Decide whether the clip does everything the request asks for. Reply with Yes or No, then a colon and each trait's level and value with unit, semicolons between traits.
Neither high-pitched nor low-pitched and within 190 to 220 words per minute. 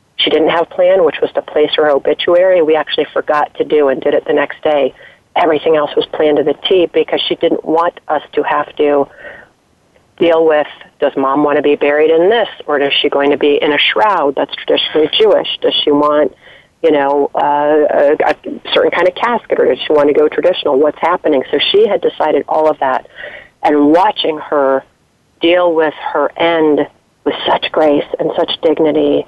Yes: medium, 160 Hz; fast, 205 wpm